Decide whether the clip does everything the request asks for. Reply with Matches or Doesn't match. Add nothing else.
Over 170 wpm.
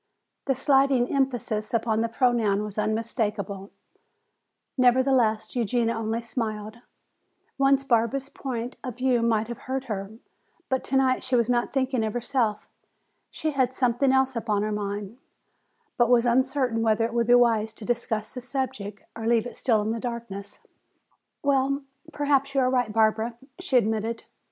Doesn't match